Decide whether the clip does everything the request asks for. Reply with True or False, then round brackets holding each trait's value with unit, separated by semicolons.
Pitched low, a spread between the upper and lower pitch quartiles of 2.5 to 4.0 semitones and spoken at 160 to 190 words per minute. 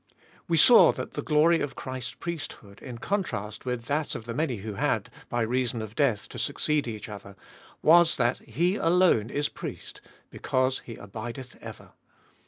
False (130 Hz; 5.5 semitones; 170 wpm)